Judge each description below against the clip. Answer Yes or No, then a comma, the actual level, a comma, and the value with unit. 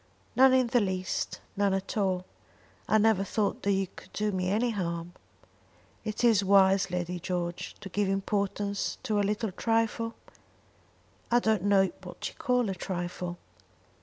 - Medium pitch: No, high, 200 Hz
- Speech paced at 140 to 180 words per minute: Yes, average, 160 wpm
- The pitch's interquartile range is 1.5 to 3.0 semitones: Yes, average, 2.7 semitones